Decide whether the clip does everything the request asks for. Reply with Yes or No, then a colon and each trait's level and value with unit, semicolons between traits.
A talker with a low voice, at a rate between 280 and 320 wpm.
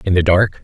Yes: very low, 90 Hz; fast, 285 wpm